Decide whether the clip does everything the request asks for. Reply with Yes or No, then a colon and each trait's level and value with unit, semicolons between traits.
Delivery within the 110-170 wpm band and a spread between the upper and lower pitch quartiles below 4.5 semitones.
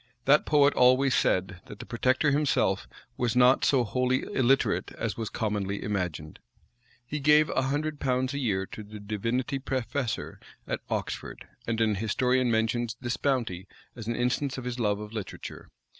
Yes: average, 165 wpm; average, 3.8 semitones